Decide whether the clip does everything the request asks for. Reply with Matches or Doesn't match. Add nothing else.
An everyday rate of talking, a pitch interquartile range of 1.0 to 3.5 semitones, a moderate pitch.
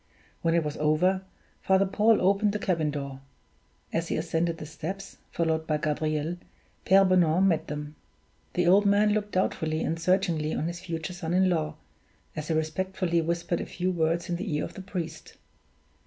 Matches